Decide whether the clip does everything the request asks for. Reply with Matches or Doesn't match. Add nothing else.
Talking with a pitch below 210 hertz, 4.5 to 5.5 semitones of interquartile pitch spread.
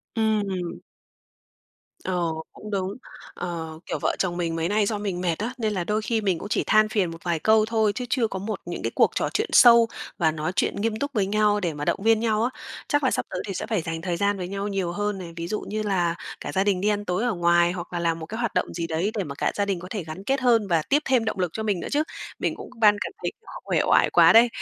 Doesn't match